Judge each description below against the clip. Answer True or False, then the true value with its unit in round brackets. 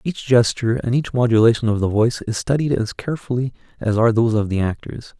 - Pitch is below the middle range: True (115 Hz)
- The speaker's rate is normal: False (210 wpm)